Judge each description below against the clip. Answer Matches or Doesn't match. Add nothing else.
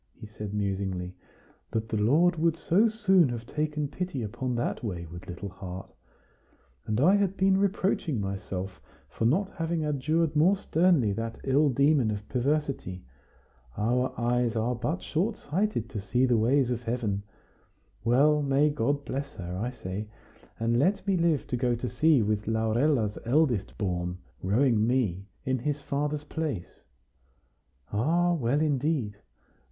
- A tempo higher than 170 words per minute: Doesn't match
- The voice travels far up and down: Matches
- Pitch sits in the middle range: Doesn't match